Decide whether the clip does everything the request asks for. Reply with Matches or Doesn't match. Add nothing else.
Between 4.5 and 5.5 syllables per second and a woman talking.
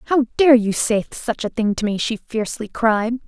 Matches